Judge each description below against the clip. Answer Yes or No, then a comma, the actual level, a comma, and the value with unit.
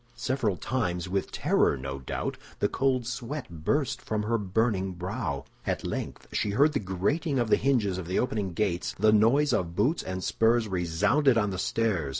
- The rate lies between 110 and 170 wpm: No, average, 180 wpm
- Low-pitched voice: Yes, low, 105 Hz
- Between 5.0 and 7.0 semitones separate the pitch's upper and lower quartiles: Yes, average, 5.3 semitones